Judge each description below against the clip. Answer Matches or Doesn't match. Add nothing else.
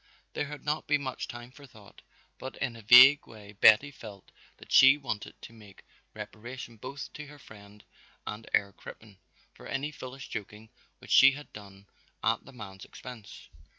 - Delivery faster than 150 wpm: Matches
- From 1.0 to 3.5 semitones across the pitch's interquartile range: Doesn't match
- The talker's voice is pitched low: Matches